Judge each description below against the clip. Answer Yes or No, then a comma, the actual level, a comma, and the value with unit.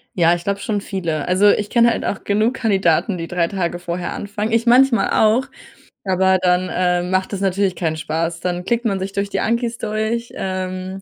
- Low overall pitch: No, high, 190 Hz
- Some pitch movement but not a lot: Yes, average, 3.2 semitones